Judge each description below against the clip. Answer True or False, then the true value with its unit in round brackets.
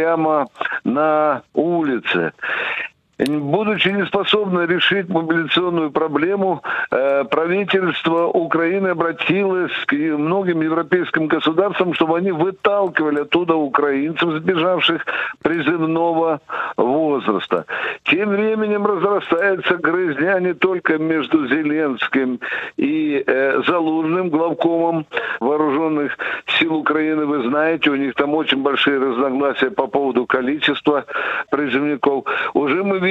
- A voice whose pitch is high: False (165 Hz)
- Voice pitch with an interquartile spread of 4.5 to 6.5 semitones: False (3.6 semitones)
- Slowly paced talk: True (95 wpm)